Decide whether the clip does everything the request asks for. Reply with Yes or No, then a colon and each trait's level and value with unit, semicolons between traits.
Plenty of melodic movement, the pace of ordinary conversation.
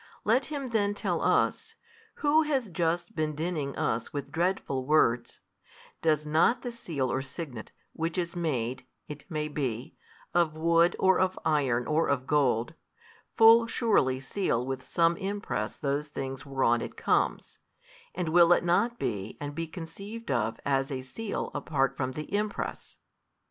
Yes: wide, 5.8 semitones; average, 160 wpm